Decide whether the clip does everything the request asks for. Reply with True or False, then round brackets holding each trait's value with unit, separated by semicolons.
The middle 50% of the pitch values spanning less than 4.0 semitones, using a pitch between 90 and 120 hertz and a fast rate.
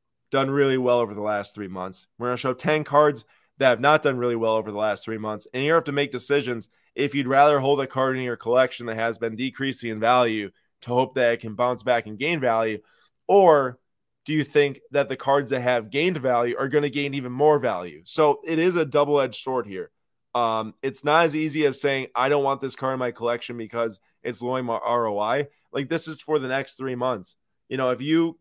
False (3.4 semitones; 130 Hz; 235 wpm)